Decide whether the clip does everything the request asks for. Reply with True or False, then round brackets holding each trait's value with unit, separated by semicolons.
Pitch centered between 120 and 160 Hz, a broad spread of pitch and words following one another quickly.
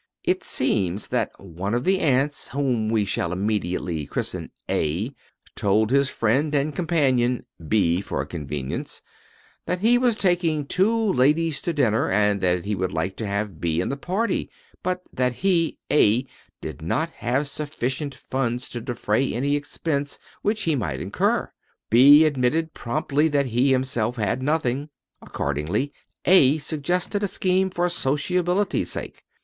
False (135 Hz; 7.0 semitones; 150 wpm)